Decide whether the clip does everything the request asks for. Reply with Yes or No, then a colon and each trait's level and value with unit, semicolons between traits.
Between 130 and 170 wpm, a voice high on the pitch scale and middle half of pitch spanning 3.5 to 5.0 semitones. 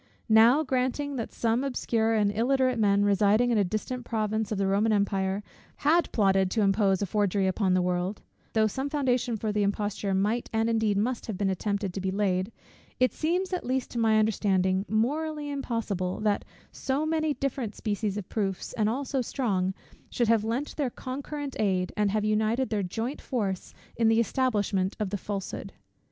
No: average, 185 wpm; high, 220 Hz; average, 4.0 semitones